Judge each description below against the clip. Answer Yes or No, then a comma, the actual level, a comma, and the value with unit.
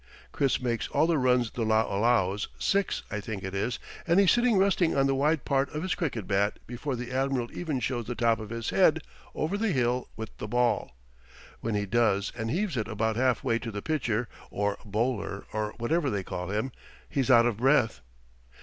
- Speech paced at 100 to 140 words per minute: No, fast, 205 wpm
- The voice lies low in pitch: Yes, low, 120 Hz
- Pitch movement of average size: Yes, average, 4.1 semitones